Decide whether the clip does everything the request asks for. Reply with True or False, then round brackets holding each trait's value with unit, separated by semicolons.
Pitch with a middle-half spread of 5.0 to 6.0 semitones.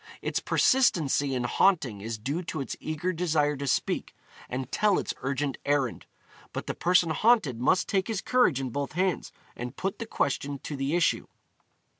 True (5.3 semitones)